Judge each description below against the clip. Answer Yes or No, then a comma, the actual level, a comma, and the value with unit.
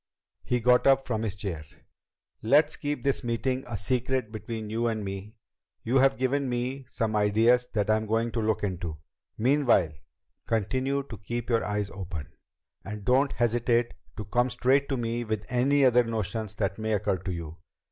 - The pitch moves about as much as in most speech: Yes, average, 3.3 semitones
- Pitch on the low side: Yes, low, 115 Hz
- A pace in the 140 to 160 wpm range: No, average, 170 wpm